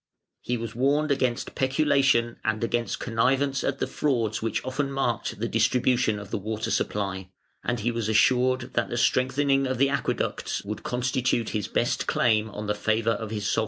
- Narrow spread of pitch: No, average, 3.2 semitones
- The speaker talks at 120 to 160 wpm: No, average, 180 wpm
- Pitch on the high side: No, low, 120 Hz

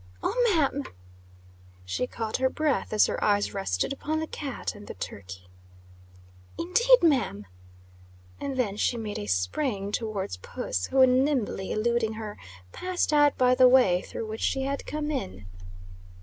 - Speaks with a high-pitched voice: Yes, high, 240 Hz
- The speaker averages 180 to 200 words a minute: No, average, 150 wpm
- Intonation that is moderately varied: No, wide, 5.8 semitones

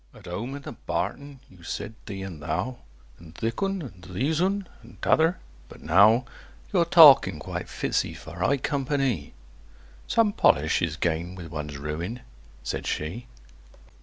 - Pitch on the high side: No, low, 100 Hz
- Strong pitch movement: Yes, wide, 8.7 semitones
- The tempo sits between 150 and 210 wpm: Yes, average, 165 wpm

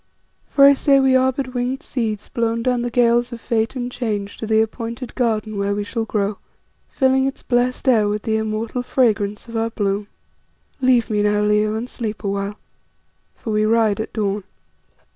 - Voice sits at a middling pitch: No, high, 225 Hz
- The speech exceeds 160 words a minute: Yes, average, 185 wpm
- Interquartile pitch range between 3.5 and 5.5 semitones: No, average, 2.8 semitones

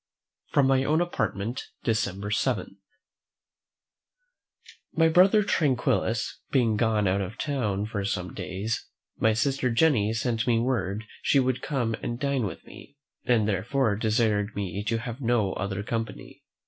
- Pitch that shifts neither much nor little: Yes, average, 4.1 semitones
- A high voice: No, low, 115 Hz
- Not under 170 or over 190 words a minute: No, average, 140 wpm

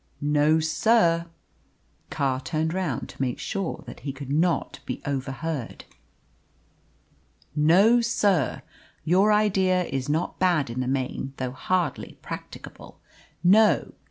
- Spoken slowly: Yes, slow, 120 wpm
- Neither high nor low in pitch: Yes, medium, 160 Hz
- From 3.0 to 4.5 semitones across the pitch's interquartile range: No, wide, 5.4 semitones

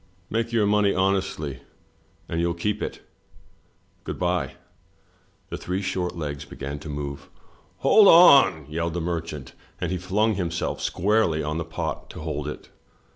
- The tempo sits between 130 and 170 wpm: Yes, average, 155 wpm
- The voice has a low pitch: Yes, very low, 85 Hz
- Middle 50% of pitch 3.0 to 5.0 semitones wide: Yes, average, 4.4 semitones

